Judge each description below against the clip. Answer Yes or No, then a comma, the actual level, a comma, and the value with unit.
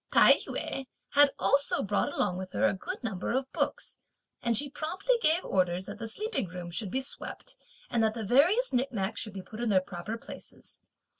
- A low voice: No, high, 230 Hz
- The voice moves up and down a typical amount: No, wide, 6.7 semitones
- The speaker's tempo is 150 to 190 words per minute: No, average, 200 wpm